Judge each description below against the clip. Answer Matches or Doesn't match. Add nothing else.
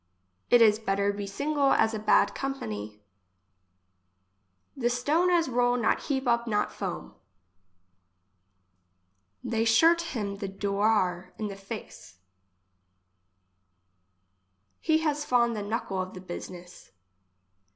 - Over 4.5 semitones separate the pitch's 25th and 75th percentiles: Matches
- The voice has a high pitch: Matches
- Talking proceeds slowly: Matches